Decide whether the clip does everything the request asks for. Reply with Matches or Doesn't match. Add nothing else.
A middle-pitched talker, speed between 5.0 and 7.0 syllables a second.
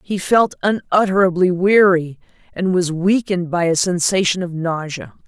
Doesn't match